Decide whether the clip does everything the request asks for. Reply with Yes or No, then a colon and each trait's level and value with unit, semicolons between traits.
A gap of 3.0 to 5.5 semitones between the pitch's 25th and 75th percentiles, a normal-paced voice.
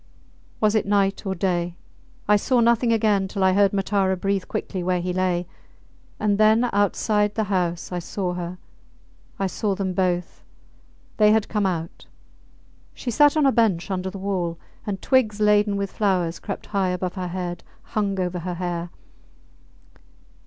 No: narrow, 2.6 semitones; average, 165 wpm